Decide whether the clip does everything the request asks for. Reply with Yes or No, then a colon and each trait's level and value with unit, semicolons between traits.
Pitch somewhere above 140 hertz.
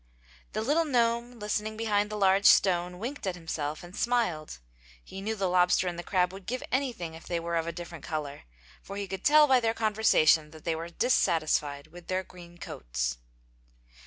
Yes: medium, 185 Hz